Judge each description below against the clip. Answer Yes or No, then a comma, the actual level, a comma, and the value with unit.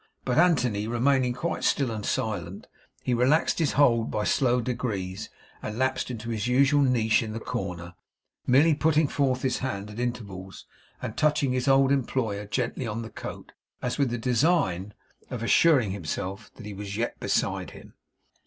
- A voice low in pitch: Yes, low, 120 Hz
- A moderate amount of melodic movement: Yes, average, 4.2 semitones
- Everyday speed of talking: Yes, average, 170 wpm